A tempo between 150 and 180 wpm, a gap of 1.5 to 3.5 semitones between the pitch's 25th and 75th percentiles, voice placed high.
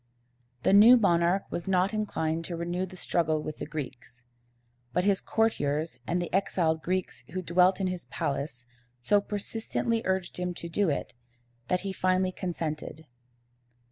No: average, 155 wpm; average, 3.2 semitones; medium, 180 Hz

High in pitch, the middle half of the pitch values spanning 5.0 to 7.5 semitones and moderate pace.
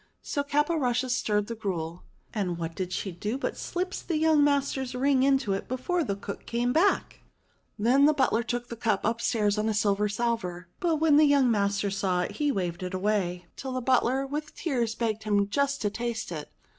Yes: high, 235 Hz; wide, 5.6 semitones; average, 195 wpm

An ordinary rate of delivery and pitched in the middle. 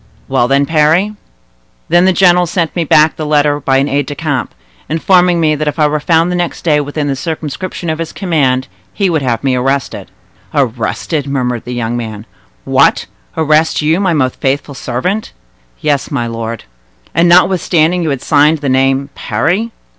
Yes: average, 175 wpm; medium, 150 Hz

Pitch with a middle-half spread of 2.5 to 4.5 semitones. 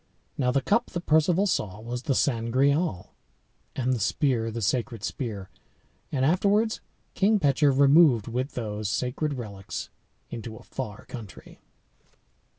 No: average, 5.1 semitones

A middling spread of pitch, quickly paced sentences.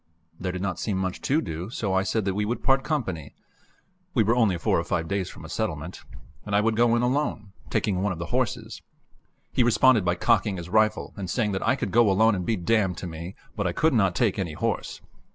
Yes: average, 4.0 semitones; fast, 240 wpm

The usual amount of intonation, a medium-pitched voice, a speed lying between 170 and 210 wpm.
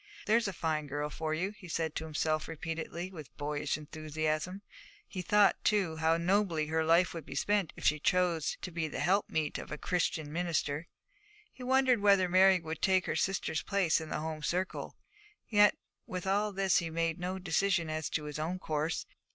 Yes: average, 3.3 semitones; medium, 165 Hz; average, 190 wpm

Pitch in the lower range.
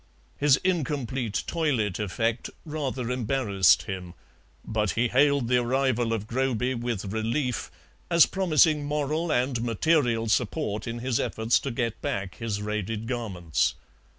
Yes: low, 120 Hz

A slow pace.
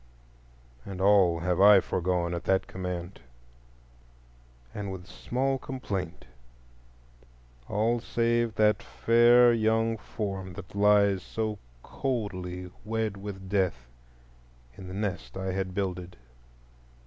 Yes: slow, 110 wpm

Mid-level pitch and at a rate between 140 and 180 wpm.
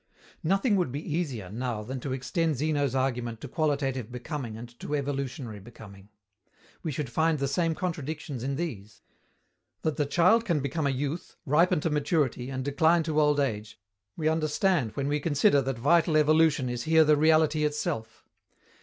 Yes: medium, 145 Hz; average, 170 wpm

